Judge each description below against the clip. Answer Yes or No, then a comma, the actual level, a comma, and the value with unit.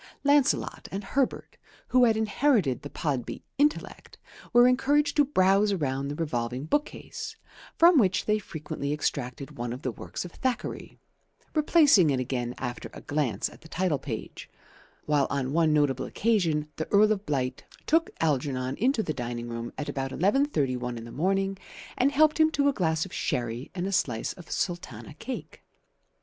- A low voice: No, medium, 160 Hz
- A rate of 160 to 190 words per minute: Yes, average, 165 wpm